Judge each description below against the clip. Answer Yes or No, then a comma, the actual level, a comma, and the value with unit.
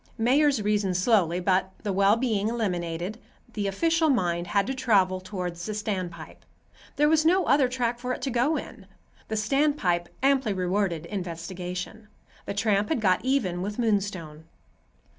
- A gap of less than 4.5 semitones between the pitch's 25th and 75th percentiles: No, average, 5.2 semitones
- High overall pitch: Yes, high, 205 Hz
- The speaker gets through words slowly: No, average, 150 wpm